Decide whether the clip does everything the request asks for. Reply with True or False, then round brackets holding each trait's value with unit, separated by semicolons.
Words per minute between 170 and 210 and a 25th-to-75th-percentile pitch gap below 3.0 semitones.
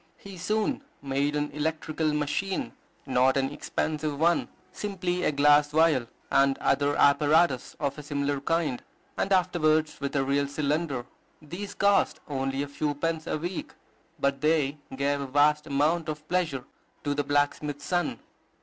False (150 wpm; 2.5 semitones)